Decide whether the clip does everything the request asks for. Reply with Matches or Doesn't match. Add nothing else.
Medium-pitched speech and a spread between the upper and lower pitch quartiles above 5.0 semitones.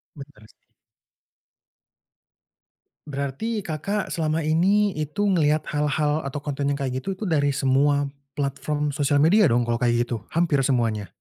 Doesn't match